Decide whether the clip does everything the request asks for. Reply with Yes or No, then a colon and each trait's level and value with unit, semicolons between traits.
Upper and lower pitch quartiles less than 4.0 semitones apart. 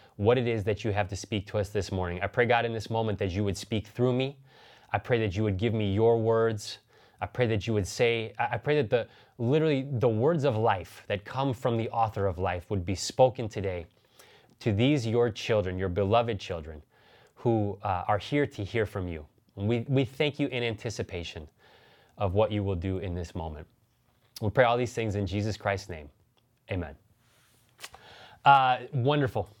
Yes: average, 3.3 semitones